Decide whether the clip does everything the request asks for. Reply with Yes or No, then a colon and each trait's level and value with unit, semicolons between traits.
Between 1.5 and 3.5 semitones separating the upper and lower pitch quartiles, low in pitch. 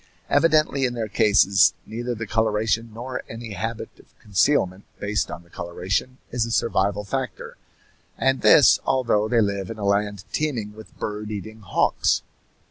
Yes: average, 2.9 semitones; low, 110 Hz